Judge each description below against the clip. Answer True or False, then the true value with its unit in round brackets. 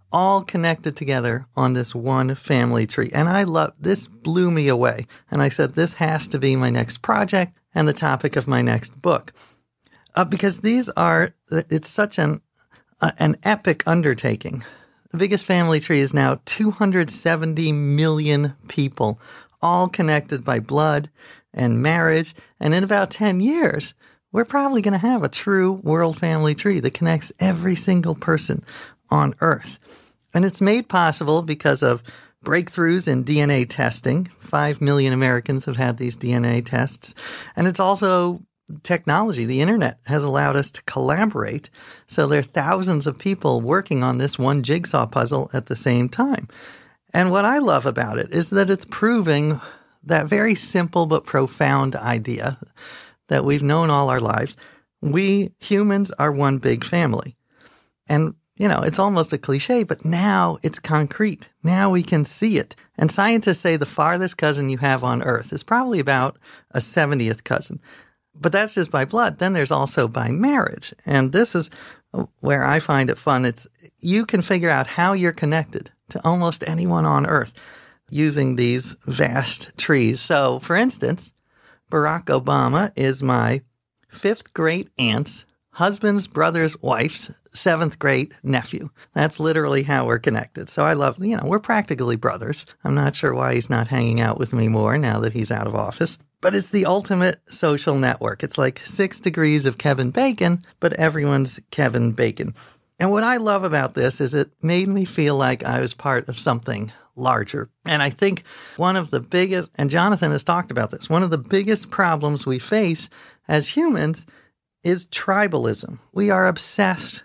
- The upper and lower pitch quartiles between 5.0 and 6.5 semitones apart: True (5.6 semitones)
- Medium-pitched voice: True (155 Hz)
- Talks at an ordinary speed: True (170 wpm)